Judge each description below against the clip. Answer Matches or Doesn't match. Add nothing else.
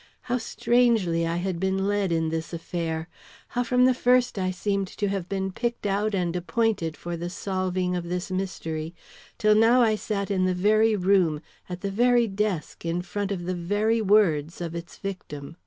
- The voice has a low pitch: Doesn't match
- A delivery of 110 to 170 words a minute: Doesn't match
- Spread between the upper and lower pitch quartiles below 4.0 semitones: Matches